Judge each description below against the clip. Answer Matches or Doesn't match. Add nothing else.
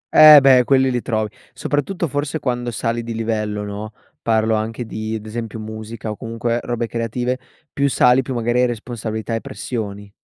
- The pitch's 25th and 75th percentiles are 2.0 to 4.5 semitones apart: Matches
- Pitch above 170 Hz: Doesn't match